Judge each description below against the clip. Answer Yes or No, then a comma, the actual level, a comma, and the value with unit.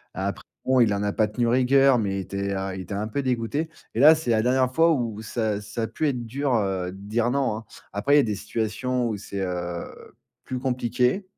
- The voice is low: Yes, low, 115 Hz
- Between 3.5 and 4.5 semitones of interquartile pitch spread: Yes, average, 4.0 semitones